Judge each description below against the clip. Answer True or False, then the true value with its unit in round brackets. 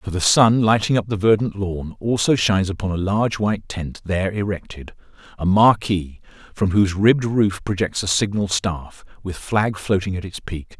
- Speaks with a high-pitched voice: False (100 Hz)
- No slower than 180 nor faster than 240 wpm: False (170 wpm)